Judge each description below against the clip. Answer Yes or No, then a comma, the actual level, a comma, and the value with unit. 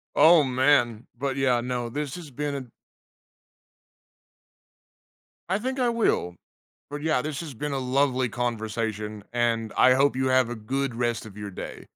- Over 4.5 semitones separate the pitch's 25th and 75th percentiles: No, average, 3.5 semitones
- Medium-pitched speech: No, low, 130 Hz